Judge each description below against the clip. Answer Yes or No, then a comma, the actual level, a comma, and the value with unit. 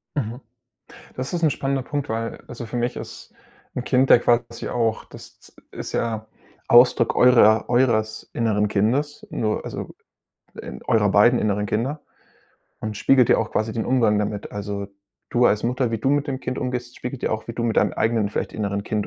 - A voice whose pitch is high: No, low, 115 Hz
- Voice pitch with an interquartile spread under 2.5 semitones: No, average, 2.8 semitones